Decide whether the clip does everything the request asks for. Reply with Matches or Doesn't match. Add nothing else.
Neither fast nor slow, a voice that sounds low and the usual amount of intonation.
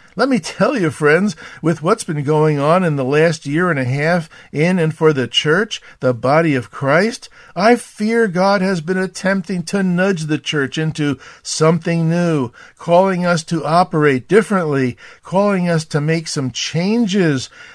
Doesn't match